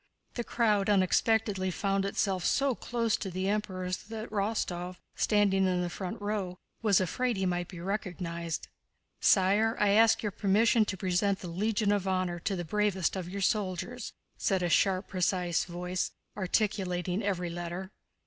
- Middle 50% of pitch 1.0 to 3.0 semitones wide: Yes, average, 2.7 semitones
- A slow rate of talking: No, average, 160 wpm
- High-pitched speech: Yes, high, 195 Hz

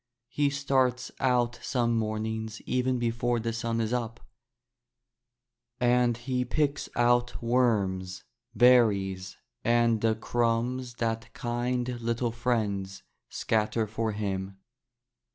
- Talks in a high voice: No, low, 115 Hz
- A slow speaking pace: Yes, slow, 105 wpm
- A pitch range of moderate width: No, narrow, 1.9 semitones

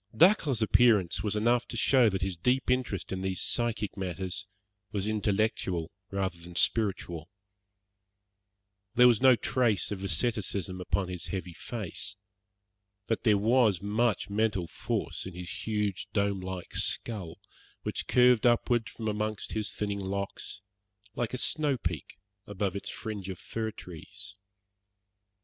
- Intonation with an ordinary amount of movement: Yes, average, 3.6 semitones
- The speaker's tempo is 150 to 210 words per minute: No, slow, 135 wpm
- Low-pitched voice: Yes, low, 105 Hz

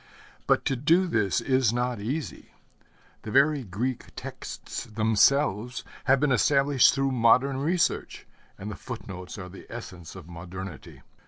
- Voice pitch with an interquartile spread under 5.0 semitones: No, wide, 5.4 semitones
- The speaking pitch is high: No, low, 120 Hz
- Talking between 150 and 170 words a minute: No, average, 140 wpm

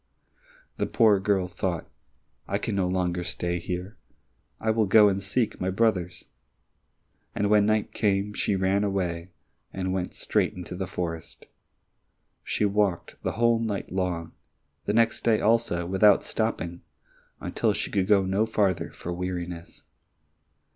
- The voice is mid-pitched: No, very low, 95 Hz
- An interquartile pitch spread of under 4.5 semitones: Yes, average, 2.7 semitones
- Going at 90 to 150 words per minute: Yes, average, 145 wpm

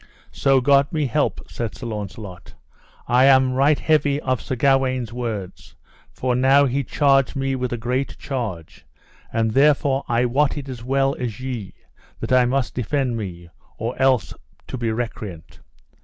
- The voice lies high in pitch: No, low, 130 Hz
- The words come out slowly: No, average, 160 wpm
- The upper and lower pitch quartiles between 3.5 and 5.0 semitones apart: No, average, 2.9 semitones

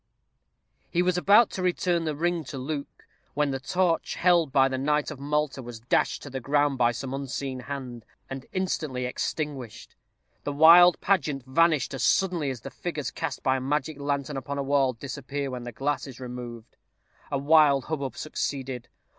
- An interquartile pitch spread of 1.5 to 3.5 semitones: Yes, average, 3.0 semitones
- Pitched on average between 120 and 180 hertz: Yes, medium, 140 Hz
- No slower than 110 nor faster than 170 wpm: No, average, 180 wpm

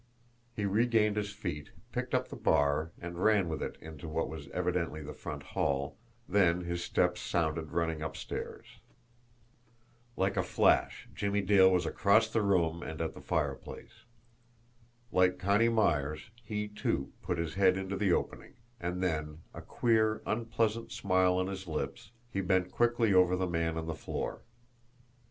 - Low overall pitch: Yes, very low, 90 Hz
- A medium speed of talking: Yes, average, 160 wpm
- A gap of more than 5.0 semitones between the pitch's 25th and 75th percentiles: No, average, 4.0 semitones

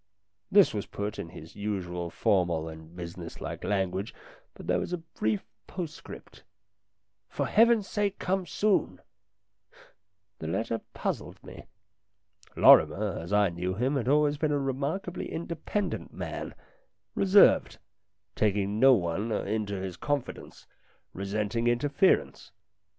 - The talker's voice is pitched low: Yes, low, 105 Hz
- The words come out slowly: Yes, slow, 125 wpm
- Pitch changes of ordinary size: No, wide, 7.9 semitones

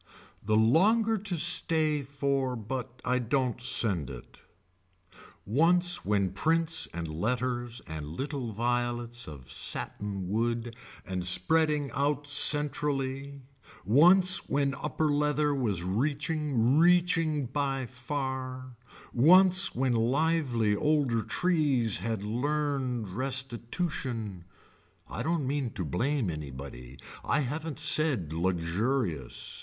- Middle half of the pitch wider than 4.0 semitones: Yes, average, 5.2 semitones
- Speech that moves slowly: Yes, slow, 105 wpm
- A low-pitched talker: Yes, low, 130 Hz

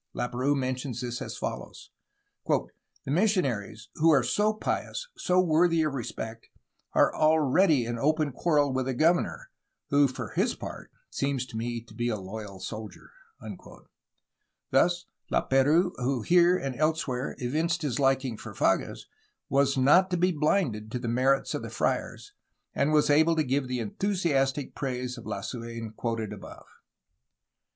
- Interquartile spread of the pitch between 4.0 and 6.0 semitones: Yes, average, 4.7 semitones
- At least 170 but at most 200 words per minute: No, average, 145 wpm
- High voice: No, low, 135 Hz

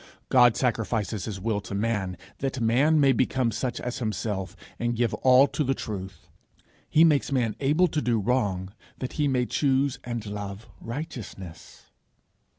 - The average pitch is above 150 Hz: No, low, 120 Hz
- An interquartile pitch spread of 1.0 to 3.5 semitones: No, average, 4.3 semitones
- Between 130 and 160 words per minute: Yes, average, 155 wpm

